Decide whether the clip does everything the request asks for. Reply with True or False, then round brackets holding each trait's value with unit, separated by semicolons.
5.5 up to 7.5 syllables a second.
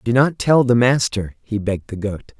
False (5.0 syllables/s)